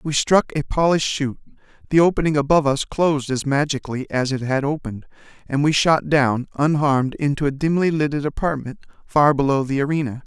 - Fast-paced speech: No, average, 175 wpm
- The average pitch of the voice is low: No, medium, 145 Hz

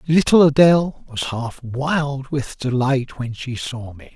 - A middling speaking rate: Yes, average, 160 wpm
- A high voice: No, low, 135 Hz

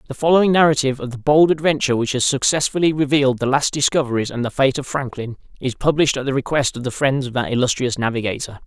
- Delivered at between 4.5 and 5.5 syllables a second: No, 6.8 syllables/s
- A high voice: No, low, 135 Hz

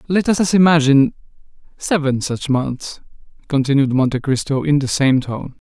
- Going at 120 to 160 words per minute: Yes, average, 140 wpm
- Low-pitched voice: No, medium, 145 Hz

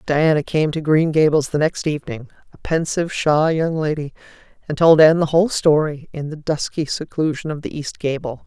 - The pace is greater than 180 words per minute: Yes, average, 190 wpm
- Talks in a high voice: No, medium, 155 Hz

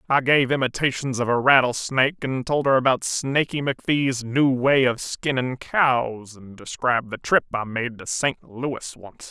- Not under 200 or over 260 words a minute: No, average, 175 wpm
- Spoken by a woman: No, male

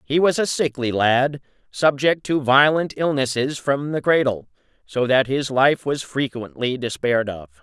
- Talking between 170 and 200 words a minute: No, average, 155 wpm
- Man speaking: Yes, male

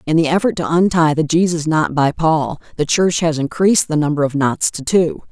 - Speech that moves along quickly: Yes, fast, 225 wpm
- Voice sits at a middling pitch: Yes, medium, 160 Hz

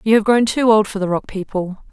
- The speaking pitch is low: No, high, 210 Hz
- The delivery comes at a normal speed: No, fast, 280 wpm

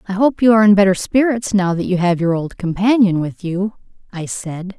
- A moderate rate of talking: No, fast, 225 wpm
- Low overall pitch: No, high, 195 Hz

